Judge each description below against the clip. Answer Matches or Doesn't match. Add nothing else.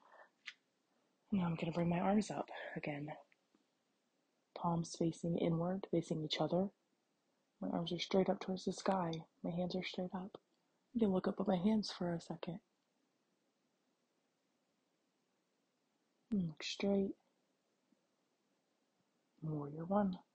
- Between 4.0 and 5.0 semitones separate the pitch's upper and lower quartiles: Doesn't match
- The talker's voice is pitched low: Doesn't match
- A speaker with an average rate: Doesn't match